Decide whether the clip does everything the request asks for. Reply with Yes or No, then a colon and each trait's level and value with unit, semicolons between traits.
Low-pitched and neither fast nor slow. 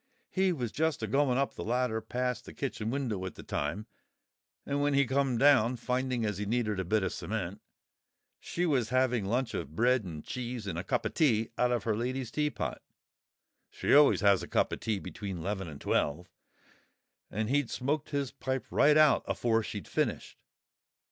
Yes: low, 120 Hz; average, 185 wpm